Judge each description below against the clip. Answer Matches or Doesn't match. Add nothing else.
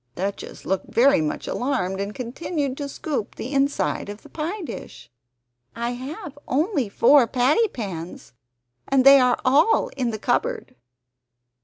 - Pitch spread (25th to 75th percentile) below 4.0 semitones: Doesn't match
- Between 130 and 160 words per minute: Matches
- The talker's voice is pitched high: Matches